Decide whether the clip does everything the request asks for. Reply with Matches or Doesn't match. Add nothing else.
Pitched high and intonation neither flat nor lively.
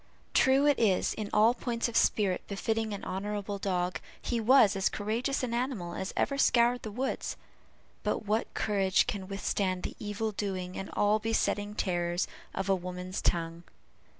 Matches